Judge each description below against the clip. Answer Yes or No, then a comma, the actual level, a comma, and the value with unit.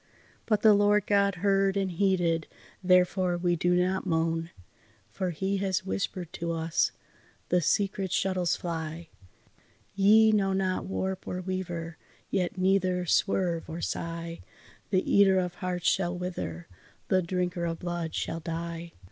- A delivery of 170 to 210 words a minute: No, average, 140 wpm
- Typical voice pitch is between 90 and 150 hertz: No, medium, 180 Hz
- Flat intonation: Yes, narrow, 2.3 semitones